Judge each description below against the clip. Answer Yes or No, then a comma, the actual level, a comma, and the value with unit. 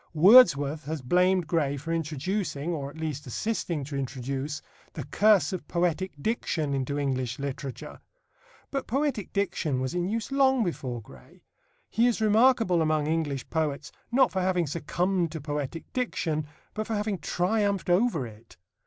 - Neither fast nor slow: Yes, average, 155 wpm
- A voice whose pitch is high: No, medium, 165 Hz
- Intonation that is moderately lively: No, wide, 6.1 semitones